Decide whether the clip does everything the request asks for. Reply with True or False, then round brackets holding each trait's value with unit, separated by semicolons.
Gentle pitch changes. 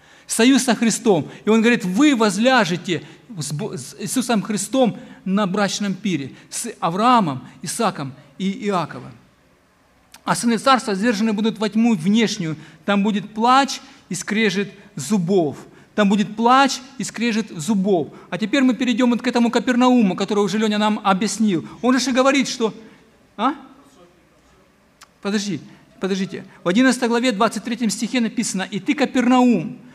False (3.8 semitones)